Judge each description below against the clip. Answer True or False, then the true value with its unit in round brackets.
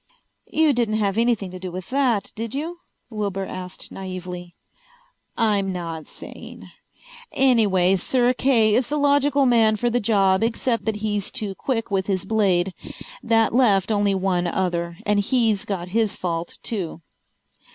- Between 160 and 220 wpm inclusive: False (150 wpm)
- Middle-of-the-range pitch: False (210 Hz)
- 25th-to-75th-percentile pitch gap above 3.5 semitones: True (3.9 semitones)